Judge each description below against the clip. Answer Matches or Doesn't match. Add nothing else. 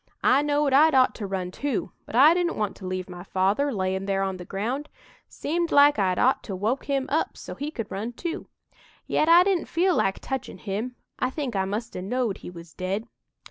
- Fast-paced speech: Matches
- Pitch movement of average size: Doesn't match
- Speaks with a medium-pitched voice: Doesn't match